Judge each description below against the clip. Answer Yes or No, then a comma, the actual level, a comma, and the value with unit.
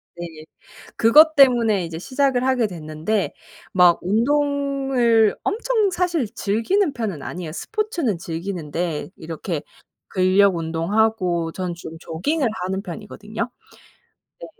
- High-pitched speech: Yes, high, 210 Hz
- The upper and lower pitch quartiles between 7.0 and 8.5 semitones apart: Yes, wide, 7.7 semitones